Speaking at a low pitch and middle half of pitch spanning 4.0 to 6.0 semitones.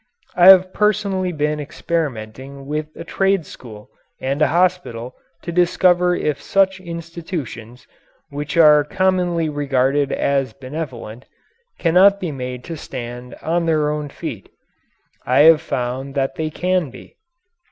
No: medium, 150 Hz; average, 4.8 semitones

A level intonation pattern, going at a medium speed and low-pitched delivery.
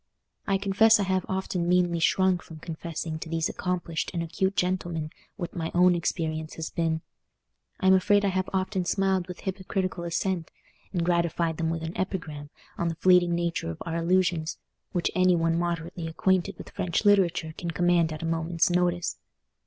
No: narrow, 2.2 semitones; average, 175 wpm; medium, 175 Hz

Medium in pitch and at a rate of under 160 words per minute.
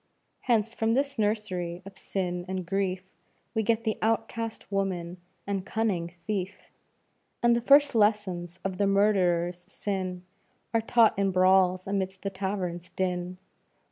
No: high, 195 Hz; average, 140 wpm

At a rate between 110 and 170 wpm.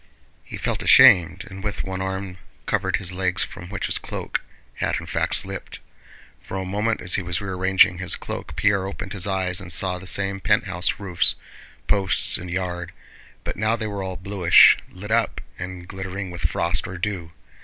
No: average, 185 wpm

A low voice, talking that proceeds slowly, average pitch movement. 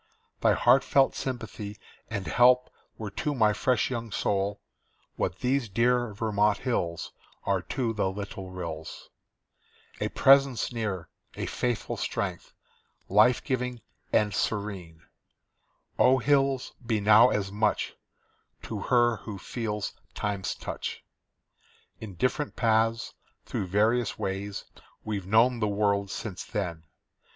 Yes: low, 110 Hz; slow, 120 wpm; average, 3.5 semitones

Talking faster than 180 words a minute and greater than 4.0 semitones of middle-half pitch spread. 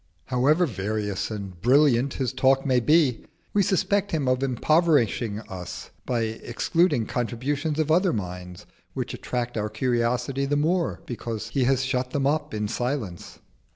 No: average, 155 wpm; average, 4.6 semitones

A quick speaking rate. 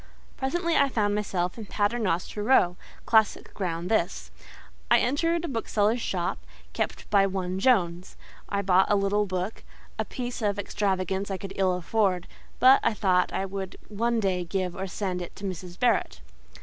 No: average, 160 wpm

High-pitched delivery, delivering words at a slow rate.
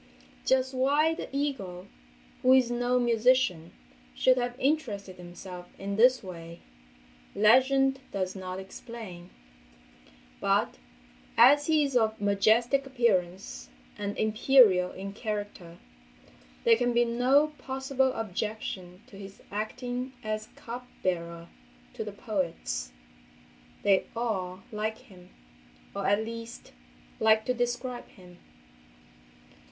Yes: high, 220 Hz; slow, 105 wpm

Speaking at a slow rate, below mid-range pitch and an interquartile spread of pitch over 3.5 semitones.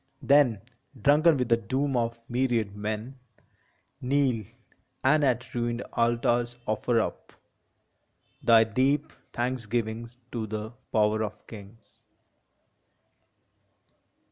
No: slow, 95 wpm; low, 120 Hz; average, 2.8 semitones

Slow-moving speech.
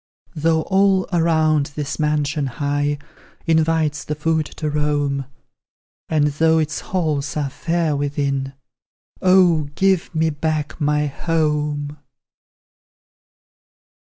Yes: slow, 100 wpm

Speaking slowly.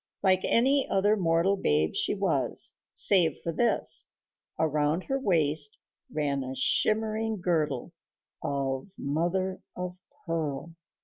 Yes: slow, 115 wpm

